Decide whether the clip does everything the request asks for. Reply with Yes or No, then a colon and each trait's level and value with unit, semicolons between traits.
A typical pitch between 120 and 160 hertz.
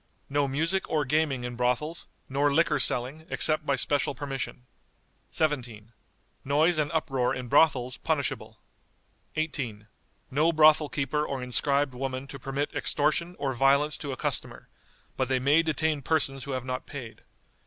Yes: medium, 140 Hz